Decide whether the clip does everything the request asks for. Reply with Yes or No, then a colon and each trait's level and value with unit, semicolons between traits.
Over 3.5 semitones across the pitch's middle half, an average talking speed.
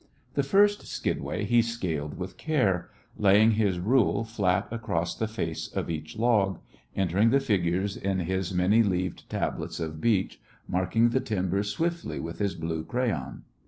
Yes: average, 4.3 semitones; average, 155 wpm